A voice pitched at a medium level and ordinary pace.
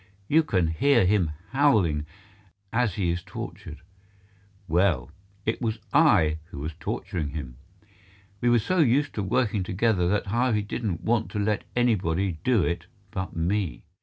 No: low, 100 Hz; average, 150 wpm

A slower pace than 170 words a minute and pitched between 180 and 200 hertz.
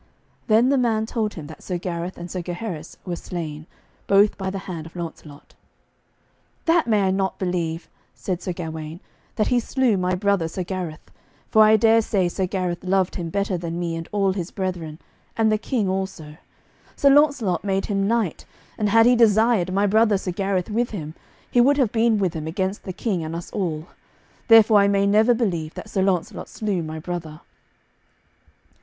No: average, 185 wpm; high, 190 Hz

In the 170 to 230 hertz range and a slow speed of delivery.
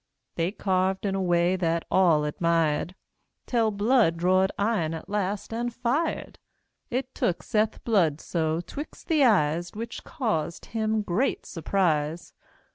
Yes: high, 190 Hz; slow, 130 wpm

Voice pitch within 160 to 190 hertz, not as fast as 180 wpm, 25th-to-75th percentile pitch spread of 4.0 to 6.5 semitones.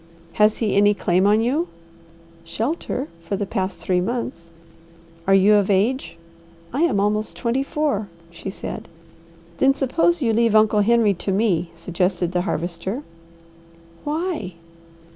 No: high, 210 Hz; average, 140 wpm; average, 4.7 semitones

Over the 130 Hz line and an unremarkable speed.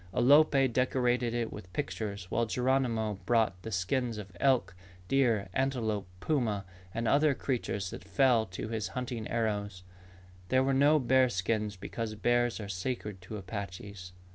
No: low, 115 Hz; average, 145 wpm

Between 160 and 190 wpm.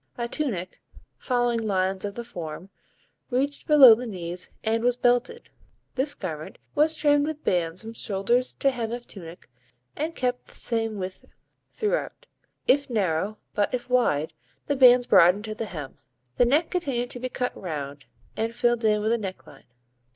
Yes: average, 165 wpm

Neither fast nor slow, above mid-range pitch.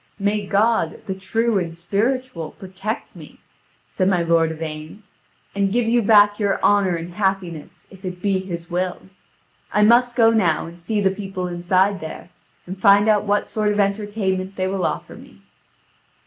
Yes: average, 170 wpm; high, 195 Hz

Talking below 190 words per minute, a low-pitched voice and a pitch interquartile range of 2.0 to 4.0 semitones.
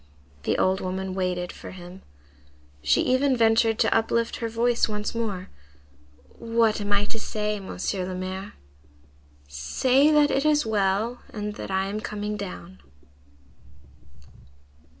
No: slow, 135 wpm; high, 210 Hz; average, 3.4 semitones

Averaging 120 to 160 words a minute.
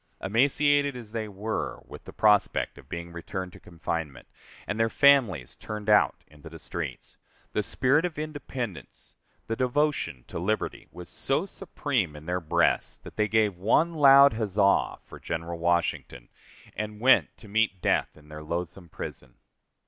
Yes: average, 155 wpm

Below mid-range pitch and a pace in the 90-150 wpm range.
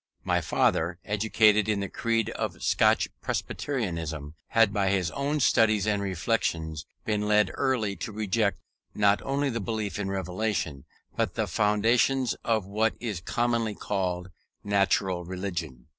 Yes: low, 105 Hz; average, 140 wpm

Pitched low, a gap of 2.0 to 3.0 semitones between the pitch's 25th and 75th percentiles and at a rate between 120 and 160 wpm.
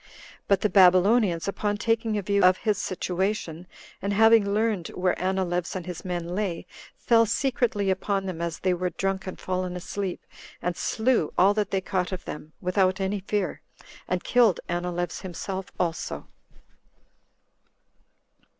No: high, 190 Hz; narrow, 2.4 semitones; average, 150 wpm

